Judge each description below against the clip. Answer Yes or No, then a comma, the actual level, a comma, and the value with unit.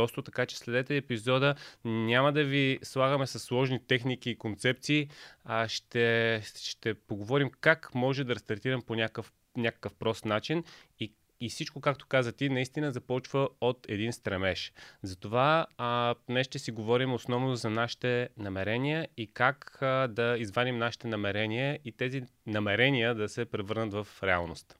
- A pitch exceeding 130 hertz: No, low, 120 Hz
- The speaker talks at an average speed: Yes, average, 150 wpm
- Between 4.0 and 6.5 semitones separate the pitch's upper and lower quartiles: No, average, 2.9 semitones